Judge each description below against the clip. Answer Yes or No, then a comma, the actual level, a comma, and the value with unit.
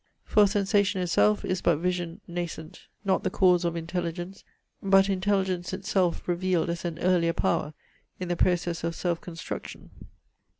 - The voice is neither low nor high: Yes, medium, 180 Hz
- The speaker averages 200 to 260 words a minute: No, average, 145 wpm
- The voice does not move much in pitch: Yes, narrow, 1.9 semitones